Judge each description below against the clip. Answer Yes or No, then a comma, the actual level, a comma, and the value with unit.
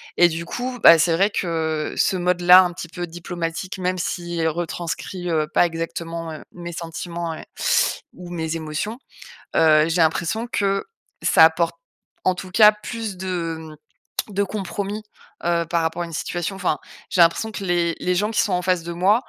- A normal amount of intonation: No, narrow, 2.1 semitones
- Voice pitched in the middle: Yes, medium, 175 Hz